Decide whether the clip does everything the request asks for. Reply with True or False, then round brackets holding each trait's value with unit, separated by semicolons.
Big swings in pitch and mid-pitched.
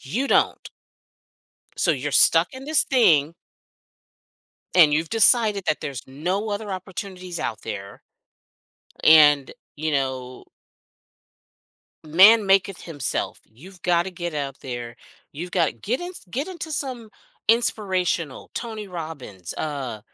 True (6.4 semitones; 170 Hz)